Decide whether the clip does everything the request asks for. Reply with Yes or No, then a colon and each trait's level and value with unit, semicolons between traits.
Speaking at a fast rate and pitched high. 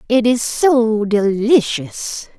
No: slow, 100 wpm; high, 225 Hz